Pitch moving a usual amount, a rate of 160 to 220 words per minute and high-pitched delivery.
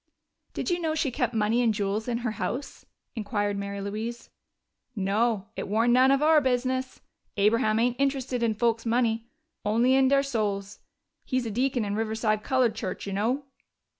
Yes: average, 3.3 semitones; average, 170 wpm; high, 230 Hz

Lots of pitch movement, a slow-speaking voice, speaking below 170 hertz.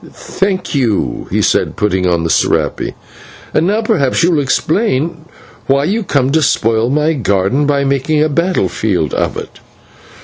No: wide, 6.1 semitones; average, 165 wpm; medium, 140 Hz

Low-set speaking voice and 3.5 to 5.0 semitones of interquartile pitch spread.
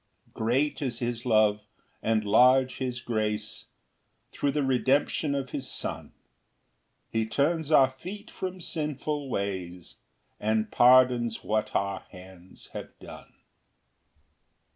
Yes: low, 120 Hz; average, 4.4 semitones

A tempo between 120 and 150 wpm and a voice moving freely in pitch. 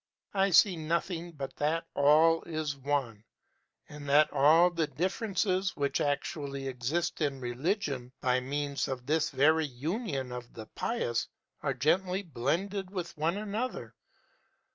No: slow, 135 wpm; average, 4.5 semitones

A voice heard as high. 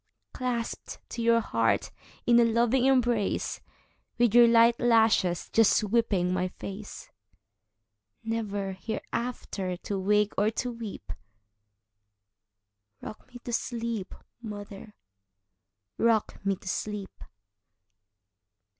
Yes: high, 205 Hz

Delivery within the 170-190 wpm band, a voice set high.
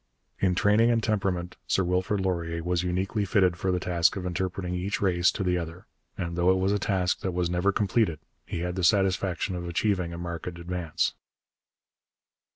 No: average, 185 wpm; very low, 90 Hz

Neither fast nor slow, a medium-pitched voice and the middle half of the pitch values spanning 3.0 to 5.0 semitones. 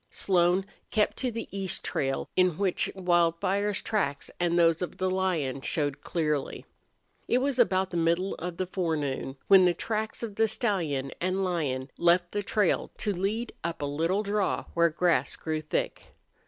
Yes: average, 170 wpm; medium, 180 Hz; average, 3.3 semitones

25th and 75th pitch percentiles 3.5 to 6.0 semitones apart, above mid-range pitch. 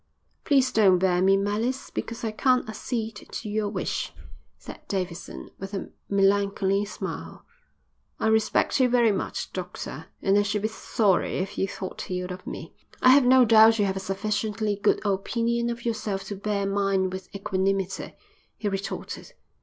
No: narrow, 2.4 semitones; high, 205 Hz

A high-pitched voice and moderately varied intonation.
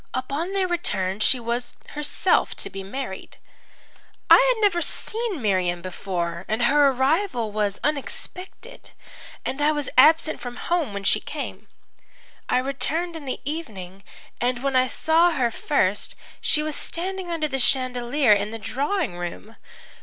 No: very high, 265 Hz; wide, 7.1 semitones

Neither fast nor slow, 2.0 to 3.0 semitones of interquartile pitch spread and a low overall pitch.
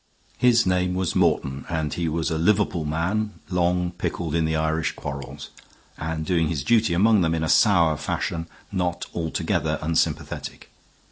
Yes: average, 155 wpm; narrow, 2.5 semitones; very low, 85 Hz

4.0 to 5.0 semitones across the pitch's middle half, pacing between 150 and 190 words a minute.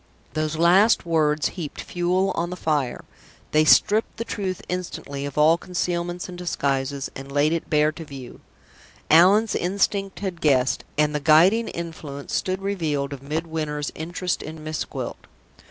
No: average, 3.4 semitones; average, 155 wpm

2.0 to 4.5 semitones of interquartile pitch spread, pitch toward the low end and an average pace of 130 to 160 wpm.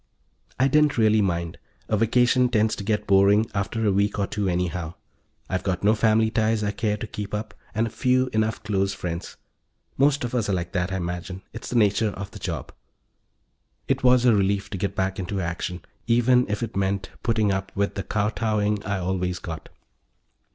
No: average, 2.7 semitones; low, 105 Hz; average, 195 wpm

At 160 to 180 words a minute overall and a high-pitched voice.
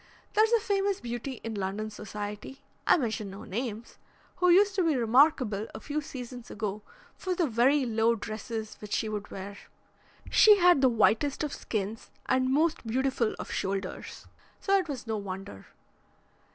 Yes: average, 165 wpm; high, 235 Hz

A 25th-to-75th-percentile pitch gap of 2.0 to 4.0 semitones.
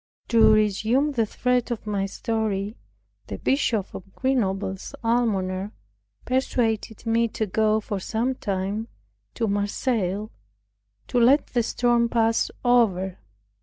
Yes: average, 3.1 semitones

